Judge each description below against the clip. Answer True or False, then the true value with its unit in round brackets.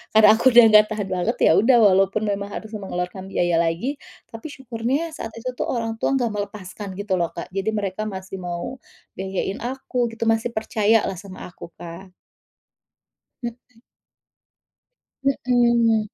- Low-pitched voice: False (215 Hz)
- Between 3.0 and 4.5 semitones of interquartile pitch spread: True (3.4 semitones)